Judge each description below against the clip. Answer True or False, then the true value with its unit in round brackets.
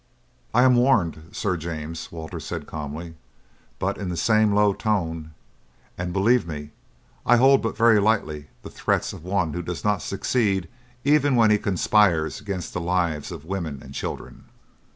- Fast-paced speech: False (165 wpm)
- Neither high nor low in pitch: False (90 Hz)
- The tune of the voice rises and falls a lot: False (4.8 semitones)